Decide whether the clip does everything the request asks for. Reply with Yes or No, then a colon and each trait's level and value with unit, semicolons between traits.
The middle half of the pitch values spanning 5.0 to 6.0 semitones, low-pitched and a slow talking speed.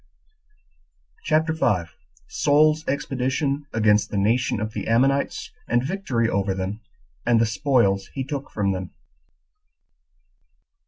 Yes: average, 5.3 semitones; low, 120 Hz; slow, 115 wpm